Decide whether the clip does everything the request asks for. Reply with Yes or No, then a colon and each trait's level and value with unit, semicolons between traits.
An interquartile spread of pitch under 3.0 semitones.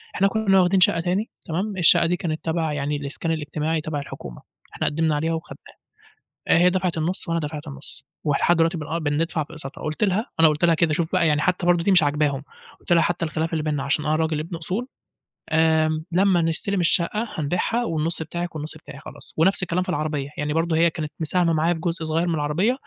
Yes: narrow, 2.4 semitones